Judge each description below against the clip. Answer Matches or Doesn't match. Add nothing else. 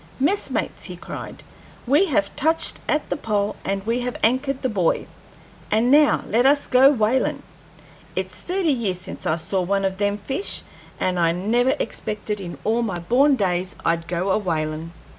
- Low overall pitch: Doesn't match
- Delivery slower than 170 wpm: Doesn't match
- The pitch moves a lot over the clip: Matches